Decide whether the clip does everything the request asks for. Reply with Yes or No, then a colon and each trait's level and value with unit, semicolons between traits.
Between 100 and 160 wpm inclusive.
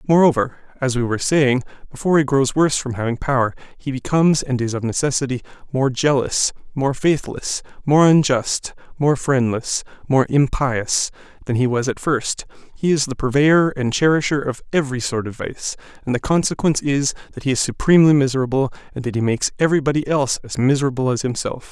No: average, 175 wpm